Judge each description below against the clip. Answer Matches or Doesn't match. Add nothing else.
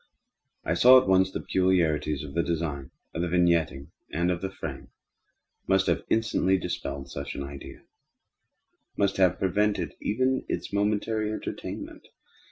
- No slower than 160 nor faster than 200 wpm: Doesn't match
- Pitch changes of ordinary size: Matches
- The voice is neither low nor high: Doesn't match